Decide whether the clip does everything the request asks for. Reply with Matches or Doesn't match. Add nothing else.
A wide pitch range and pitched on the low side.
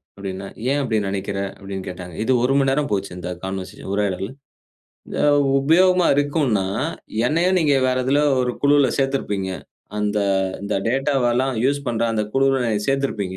Matches